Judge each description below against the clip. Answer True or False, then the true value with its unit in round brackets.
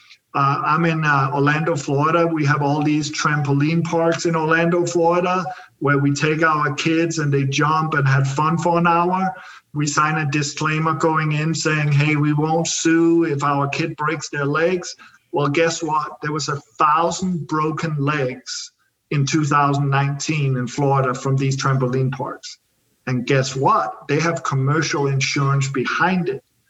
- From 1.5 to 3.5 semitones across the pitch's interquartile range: True (2.6 semitones)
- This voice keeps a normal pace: True (160 wpm)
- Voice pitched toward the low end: False (150 Hz)